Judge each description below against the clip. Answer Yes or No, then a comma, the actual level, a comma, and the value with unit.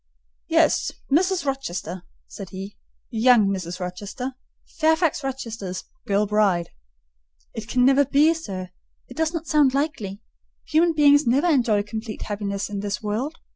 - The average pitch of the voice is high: Yes, high, 230 Hz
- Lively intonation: Yes, wide, 6.4 semitones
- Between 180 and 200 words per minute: No, slow, 135 wpm